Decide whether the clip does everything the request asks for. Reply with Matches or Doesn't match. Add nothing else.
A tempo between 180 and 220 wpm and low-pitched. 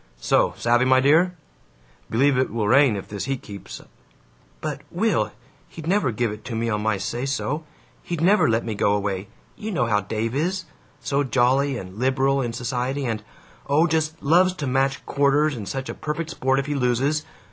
Matches